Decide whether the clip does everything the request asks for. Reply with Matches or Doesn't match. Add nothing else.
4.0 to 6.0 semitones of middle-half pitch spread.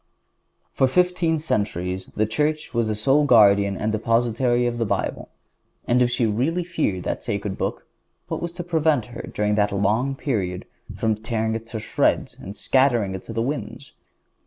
Matches